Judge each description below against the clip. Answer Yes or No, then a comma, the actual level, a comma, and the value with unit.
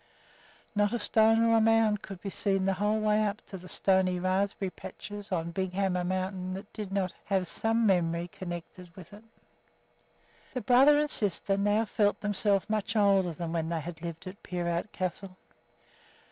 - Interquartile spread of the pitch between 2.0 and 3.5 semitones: Yes, narrow, 2.5 semitones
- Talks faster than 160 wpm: Yes, average, 175 wpm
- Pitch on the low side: No, high, 195 Hz